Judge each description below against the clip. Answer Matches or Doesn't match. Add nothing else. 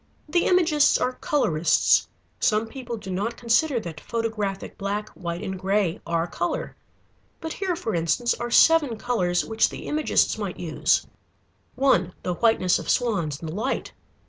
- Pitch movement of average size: Doesn't match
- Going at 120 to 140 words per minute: Doesn't match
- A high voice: Matches